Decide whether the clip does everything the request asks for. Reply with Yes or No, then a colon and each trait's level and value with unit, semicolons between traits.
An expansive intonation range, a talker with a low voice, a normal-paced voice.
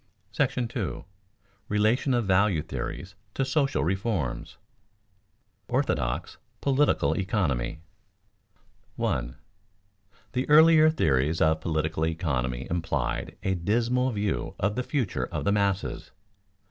No: wide, 7.4 semitones; very low, 95 Hz; slow, 110 wpm